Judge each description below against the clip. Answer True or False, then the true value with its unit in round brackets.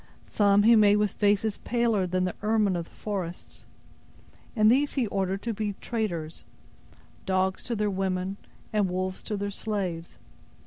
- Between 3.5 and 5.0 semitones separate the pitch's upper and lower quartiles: False (2.4 semitones)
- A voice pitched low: False (200 Hz)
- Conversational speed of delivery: True (160 wpm)